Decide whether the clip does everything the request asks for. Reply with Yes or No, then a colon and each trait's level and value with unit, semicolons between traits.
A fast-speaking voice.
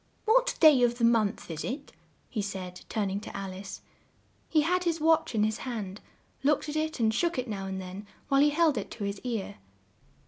Yes: fast, 215 wpm